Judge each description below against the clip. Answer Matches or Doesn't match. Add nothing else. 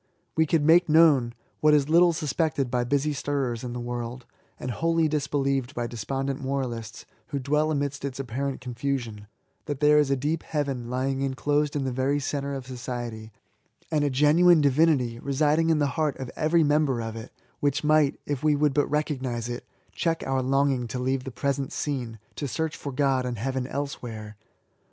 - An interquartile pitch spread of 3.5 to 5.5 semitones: Doesn't match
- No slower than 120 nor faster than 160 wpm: Doesn't match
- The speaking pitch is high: Doesn't match